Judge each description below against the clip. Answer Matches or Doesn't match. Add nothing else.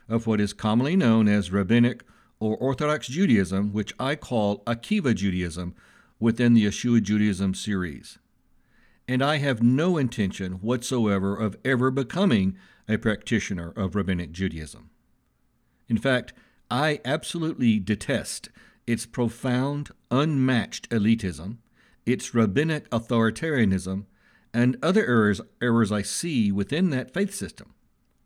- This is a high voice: Doesn't match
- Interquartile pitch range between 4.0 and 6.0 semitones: Matches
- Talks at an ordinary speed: Doesn't match